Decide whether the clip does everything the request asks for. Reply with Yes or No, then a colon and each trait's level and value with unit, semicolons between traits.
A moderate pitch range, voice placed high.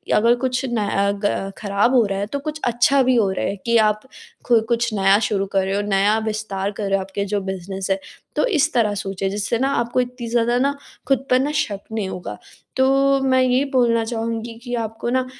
Yes: average, 4.1 semitones; high, 225 Hz